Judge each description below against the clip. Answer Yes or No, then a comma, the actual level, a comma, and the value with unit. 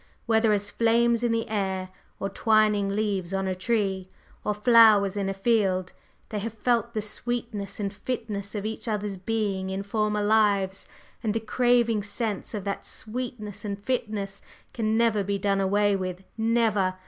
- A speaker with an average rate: Yes, average, 165 wpm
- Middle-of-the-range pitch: No, high, 210 Hz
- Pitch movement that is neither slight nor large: No, narrow, 2.3 semitones